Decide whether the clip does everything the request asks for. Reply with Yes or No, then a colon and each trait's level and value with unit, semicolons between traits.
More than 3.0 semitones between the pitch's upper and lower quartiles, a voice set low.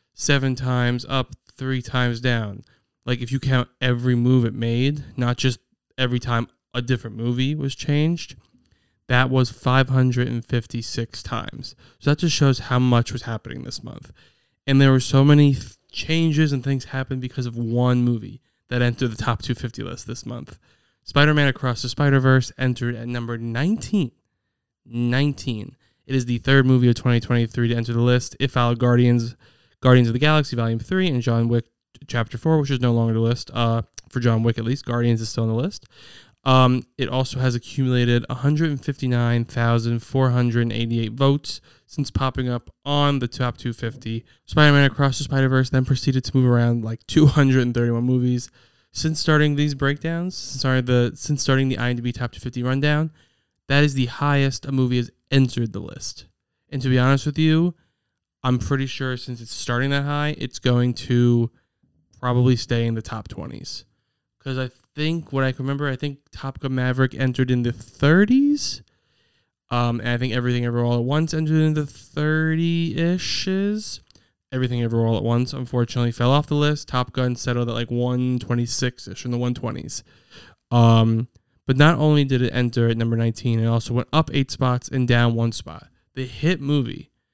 No: narrow, 2.5 semitones; low, 125 Hz